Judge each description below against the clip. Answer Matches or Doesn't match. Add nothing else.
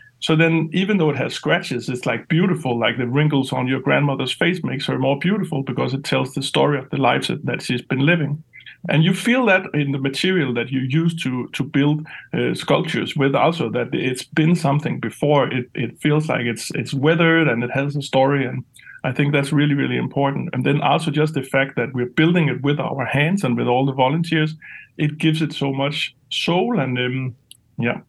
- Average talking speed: Doesn't match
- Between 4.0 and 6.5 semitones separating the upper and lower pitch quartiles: Doesn't match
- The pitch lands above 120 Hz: Matches